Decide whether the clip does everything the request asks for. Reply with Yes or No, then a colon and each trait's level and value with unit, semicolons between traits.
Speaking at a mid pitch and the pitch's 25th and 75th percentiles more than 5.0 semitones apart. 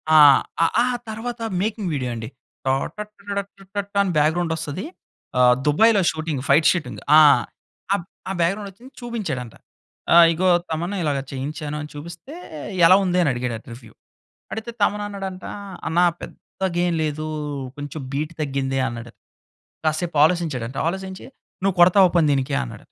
Yes: medium, 170 Hz; wide, 5.4 semitones